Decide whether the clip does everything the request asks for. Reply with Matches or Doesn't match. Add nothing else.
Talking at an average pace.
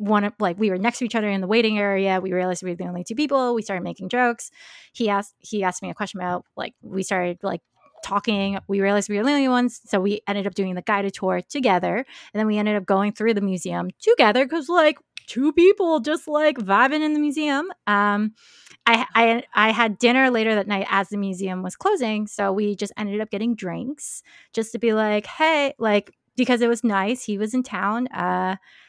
Doesn't match